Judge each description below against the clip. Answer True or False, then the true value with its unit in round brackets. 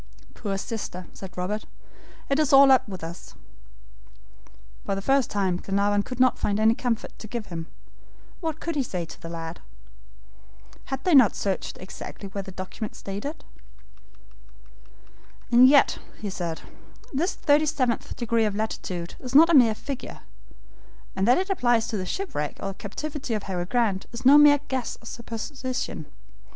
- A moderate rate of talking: True (165 wpm)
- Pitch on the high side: True (225 Hz)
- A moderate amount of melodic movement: False (5.7 semitones)